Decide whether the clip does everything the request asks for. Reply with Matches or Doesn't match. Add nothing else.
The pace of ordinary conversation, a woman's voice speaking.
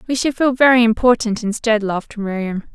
Matches